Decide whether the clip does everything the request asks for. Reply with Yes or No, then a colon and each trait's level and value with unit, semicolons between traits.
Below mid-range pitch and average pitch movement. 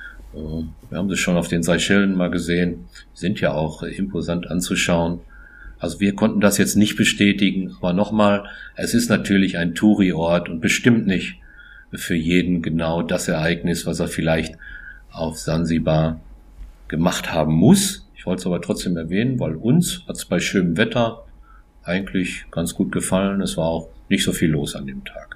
Yes: very low, 85 Hz; average, 3.1 semitones